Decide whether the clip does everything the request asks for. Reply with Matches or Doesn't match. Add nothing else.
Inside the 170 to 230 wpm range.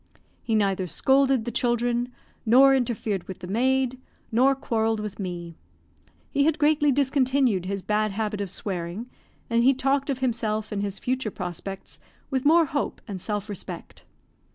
Doesn't match